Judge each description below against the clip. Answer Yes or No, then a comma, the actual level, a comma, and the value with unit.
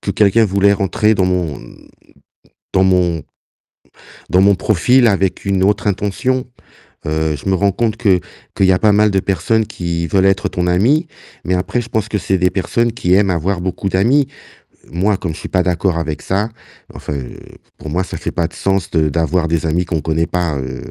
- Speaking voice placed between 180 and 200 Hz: No, very low, 95 Hz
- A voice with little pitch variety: No, average, 3.0 semitones